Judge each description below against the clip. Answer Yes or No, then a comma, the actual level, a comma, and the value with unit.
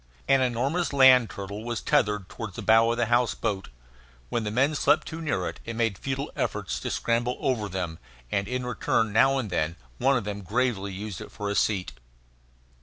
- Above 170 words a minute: Yes, average, 200 wpm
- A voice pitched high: No, low, 115 Hz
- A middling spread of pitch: Yes, average, 4.0 semitones